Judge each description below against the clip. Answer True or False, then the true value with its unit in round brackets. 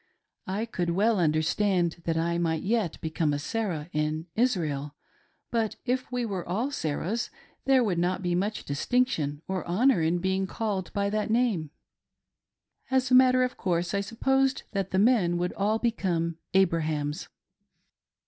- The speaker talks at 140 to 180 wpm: True (155 wpm)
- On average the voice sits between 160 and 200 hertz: True (190 Hz)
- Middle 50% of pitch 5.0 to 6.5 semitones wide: True (5.4 semitones)